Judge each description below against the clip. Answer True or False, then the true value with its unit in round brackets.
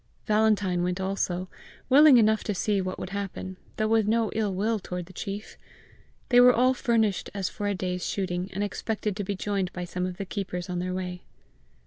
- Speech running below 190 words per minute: False (200 wpm)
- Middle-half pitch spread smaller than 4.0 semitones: True (2.9 semitones)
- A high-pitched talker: True (195 Hz)